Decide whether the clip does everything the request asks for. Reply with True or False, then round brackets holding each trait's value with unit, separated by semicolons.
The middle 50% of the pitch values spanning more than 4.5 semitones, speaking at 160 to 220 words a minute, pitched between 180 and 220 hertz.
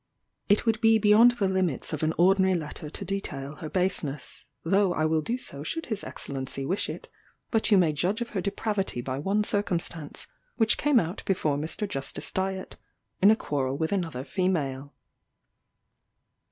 True (5.3 semitones; 170 wpm; 185 Hz)